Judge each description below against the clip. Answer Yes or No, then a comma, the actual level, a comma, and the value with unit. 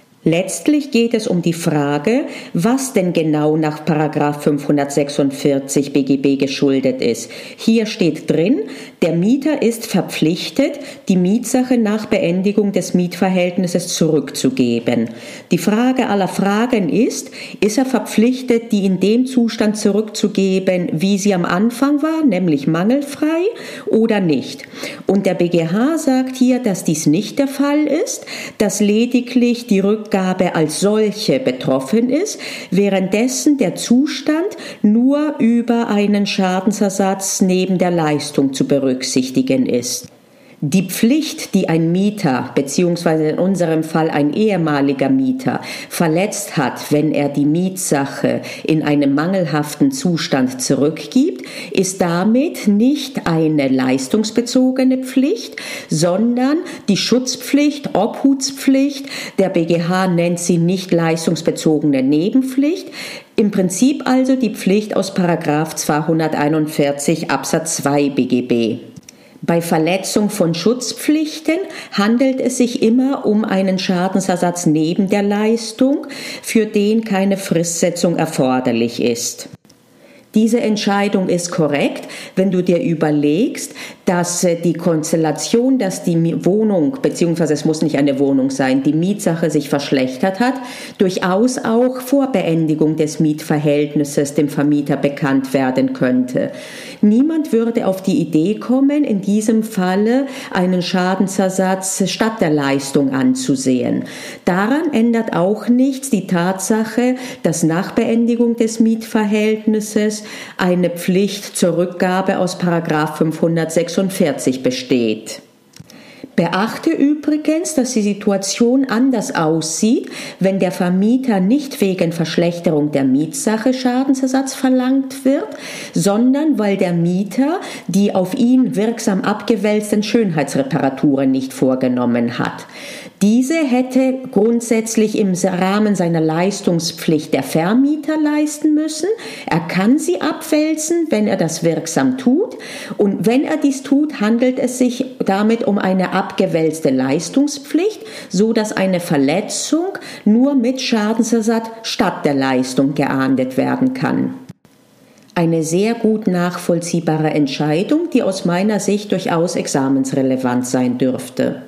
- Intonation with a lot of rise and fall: Yes, wide, 7.7 semitones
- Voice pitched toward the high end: Yes, high, 200 Hz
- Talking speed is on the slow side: Yes, slow, 115 wpm